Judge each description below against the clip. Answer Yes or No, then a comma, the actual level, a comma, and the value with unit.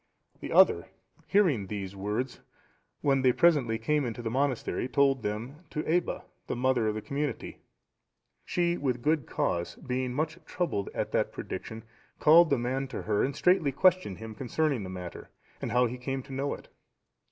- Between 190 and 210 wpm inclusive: No, average, 175 wpm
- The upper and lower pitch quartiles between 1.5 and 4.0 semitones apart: No, average, 5.0 semitones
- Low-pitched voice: Yes, low, 130 Hz